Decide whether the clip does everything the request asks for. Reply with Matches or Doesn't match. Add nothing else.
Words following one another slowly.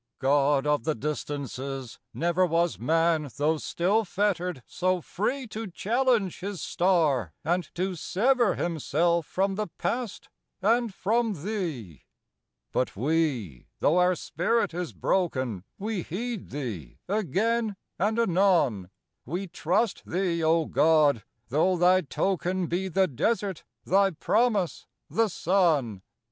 Matches